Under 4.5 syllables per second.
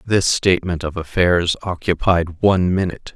No: 5.0 syllables/s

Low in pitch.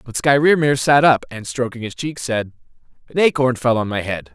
Yes: low, 125 Hz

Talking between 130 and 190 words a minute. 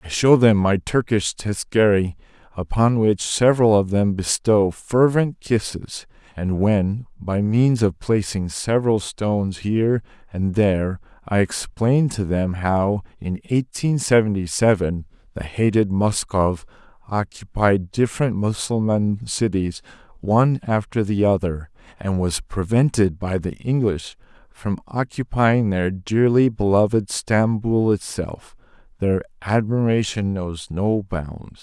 No: slow, 120 wpm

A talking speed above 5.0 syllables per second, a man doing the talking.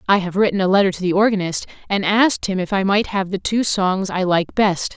No: 5.7 syllables/s; female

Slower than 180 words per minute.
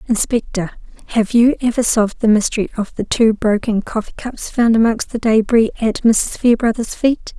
Yes: average, 170 wpm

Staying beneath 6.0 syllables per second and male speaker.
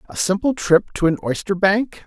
Yes: 5.1 syllables/s; male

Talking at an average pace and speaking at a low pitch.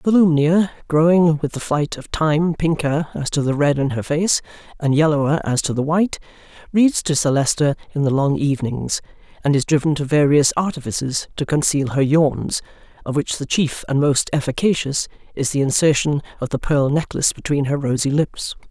No: average, 185 wpm; medium, 150 Hz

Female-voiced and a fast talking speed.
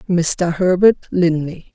No: female; slow, 105 wpm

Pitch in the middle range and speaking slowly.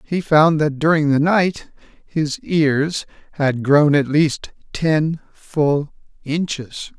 Yes: medium, 150 Hz; slow, 130 wpm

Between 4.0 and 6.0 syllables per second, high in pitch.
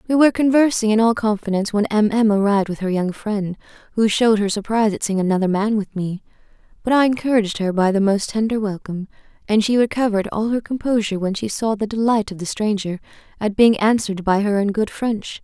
No: 6.2 syllables/s; high, 210 Hz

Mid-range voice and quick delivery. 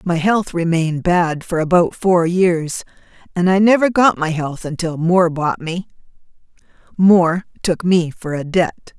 No: medium, 175 Hz; average, 160 wpm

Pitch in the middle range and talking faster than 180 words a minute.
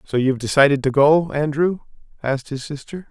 No: medium, 145 Hz; average, 175 wpm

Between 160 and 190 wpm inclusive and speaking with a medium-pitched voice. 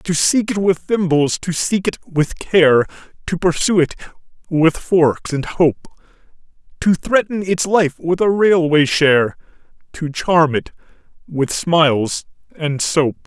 No: average, 145 wpm; medium, 165 Hz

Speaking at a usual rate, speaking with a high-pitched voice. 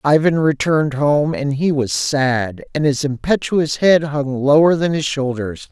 No: average, 170 wpm; medium, 145 Hz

